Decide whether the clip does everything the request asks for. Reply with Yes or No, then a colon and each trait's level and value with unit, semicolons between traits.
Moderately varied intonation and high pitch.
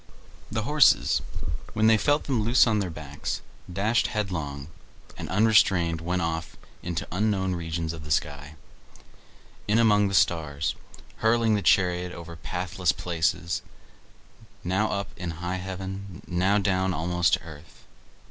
No: average, 3.8 semitones; very low, 90 Hz